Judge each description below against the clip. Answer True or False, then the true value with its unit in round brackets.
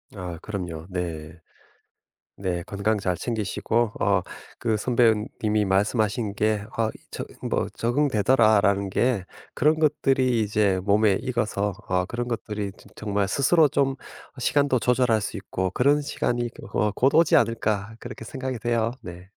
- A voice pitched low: True (110 Hz)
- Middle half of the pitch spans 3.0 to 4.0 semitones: True (3.5 semitones)